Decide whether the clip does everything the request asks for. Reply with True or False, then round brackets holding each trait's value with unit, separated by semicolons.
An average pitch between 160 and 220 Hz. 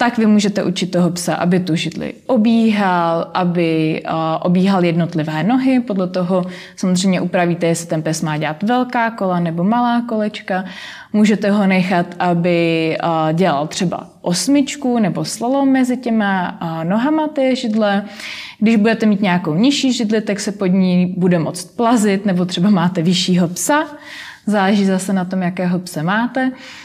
True (190 Hz)